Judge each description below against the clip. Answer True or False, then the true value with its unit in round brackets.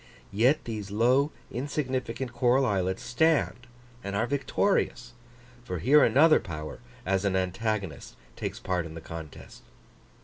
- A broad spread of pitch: True (5.7 semitones)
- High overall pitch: False (115 Hz)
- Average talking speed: False (130 wpm)